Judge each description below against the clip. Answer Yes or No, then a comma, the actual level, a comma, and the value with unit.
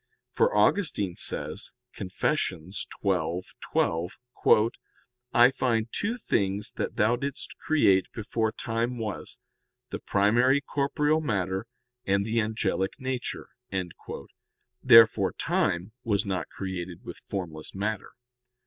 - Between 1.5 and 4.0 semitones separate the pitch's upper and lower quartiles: No, average, 4.7 semitones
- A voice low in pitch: Yes, low, 110 Hz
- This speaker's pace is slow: Yes, slow, 105 wpm